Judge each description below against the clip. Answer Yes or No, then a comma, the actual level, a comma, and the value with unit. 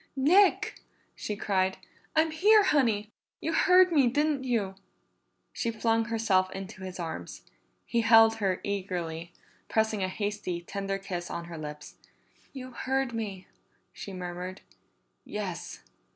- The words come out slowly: Yes, slow, 130 wpm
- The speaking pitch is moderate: No, high, 210 Hz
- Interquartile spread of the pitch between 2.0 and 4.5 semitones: No, average, 5.1 semitones